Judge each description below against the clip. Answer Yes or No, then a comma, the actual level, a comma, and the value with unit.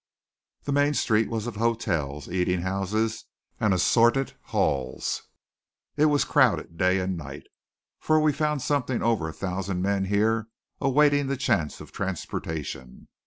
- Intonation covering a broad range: Yes, wide, 6.5 semitones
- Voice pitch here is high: No, low, 105 Hz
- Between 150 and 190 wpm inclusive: No, average, 140 wpm